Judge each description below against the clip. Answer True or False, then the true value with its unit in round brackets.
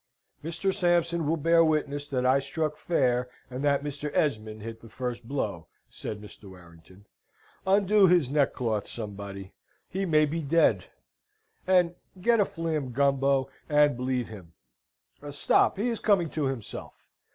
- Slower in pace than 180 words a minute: True (145 wpm)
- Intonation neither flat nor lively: False (6.2 semitones)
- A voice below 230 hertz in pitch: True (140 Hz)